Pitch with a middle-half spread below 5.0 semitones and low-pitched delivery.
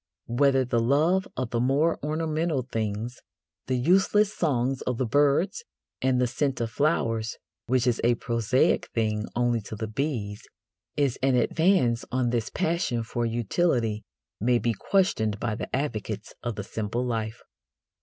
Yes: average, 4.0 semitones; low, 125 Hz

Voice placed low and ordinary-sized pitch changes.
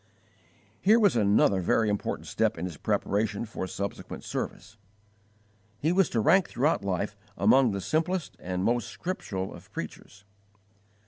No: low, 110 Hz; wide, 8.2 semitones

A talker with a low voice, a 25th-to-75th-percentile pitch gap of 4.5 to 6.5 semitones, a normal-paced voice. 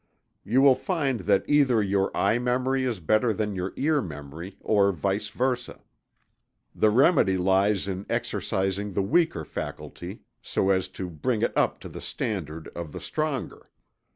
Yes: low, 105 Hz; average, 5.1 semitones; average, 160 wpm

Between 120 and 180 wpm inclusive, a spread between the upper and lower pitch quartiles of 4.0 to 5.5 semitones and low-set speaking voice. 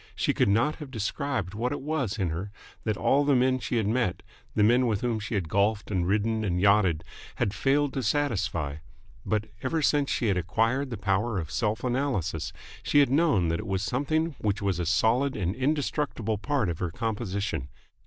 No: average, 200 wpm; average, 5.2 semitones; low, 110 Hz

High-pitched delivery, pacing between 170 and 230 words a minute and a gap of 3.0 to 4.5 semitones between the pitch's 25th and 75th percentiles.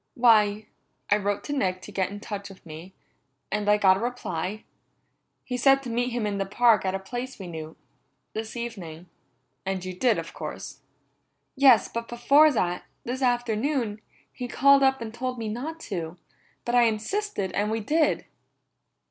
Yes: high, 220 Hz; average, 175 wpm; average, 4.2 semitones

